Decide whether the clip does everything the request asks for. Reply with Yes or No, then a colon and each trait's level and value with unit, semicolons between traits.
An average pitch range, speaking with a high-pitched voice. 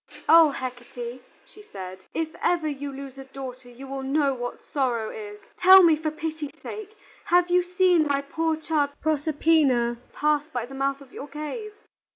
Yes: average, 3.8 semitones; very high, 285 Hz